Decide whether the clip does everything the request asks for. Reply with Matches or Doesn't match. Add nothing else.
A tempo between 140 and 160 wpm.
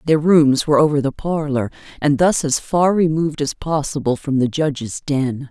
Doesn't match